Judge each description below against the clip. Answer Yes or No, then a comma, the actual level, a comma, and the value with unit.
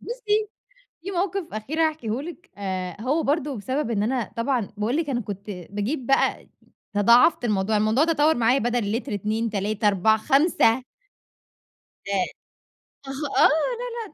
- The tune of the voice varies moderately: No, wide, 6.4 semitones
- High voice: Yes, high, 240 Hz